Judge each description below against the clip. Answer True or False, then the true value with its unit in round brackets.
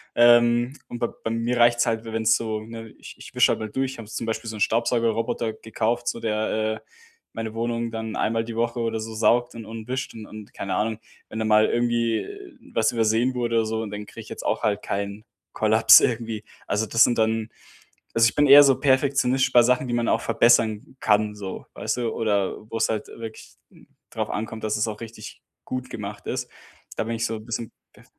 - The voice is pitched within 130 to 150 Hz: False (115 Hz)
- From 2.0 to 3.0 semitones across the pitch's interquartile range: False (1.4 semitones)